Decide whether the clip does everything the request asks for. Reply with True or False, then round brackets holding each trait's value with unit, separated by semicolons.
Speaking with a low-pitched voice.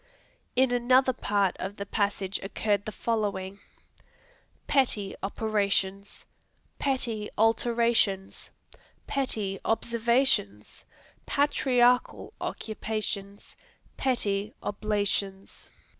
False (215 Hz)